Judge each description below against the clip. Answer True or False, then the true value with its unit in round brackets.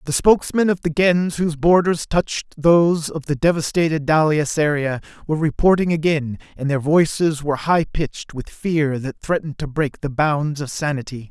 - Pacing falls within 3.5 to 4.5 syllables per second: False (5.1 syllables/s)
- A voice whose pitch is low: False (155 Hz)